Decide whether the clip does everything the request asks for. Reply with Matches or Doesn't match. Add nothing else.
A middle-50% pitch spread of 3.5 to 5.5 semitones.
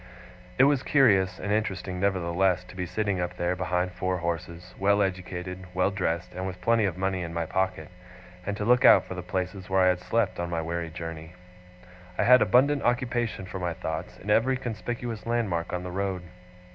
Doesn't match